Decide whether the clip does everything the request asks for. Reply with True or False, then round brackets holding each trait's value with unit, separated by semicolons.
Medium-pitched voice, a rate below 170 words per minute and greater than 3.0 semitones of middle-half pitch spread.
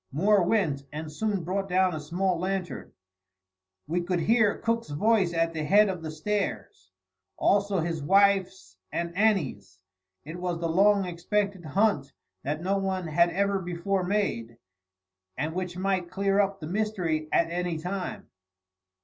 True (180 Hz; 150 wpm; 3.5 semitones)